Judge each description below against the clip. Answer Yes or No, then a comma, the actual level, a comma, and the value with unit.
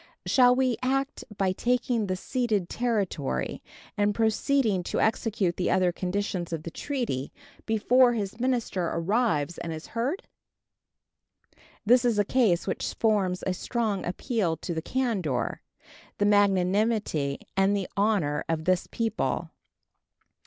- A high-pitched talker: Yes, high, 205 Hz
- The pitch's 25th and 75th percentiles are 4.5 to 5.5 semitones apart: Yes, average, 4.9 semitones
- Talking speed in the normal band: No, slow, 130 wpm